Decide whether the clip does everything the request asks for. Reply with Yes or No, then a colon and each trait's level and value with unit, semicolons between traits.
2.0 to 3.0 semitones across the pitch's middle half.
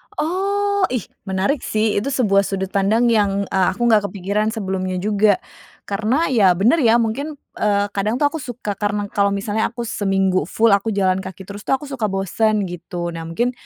No: average, 3.6 semitones